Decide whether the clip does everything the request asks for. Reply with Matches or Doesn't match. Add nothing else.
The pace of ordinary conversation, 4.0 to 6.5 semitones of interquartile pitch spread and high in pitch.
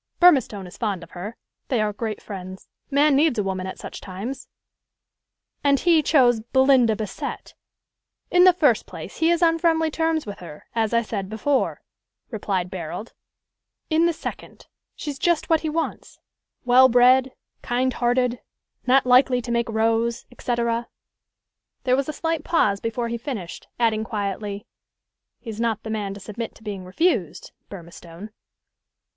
Matches